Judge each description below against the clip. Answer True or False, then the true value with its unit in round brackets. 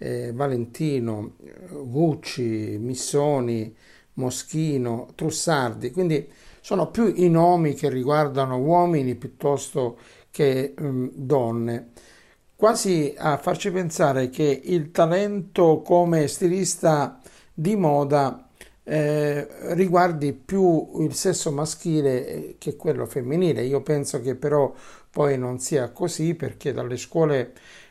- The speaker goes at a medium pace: False (105 wpm)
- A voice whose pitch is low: False (145 Hz)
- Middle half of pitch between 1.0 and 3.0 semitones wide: False (4.4 semitones)